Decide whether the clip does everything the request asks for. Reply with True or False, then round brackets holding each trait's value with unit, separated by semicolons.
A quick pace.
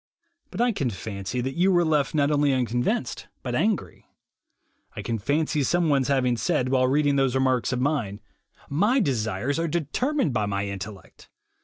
False (165 wpm)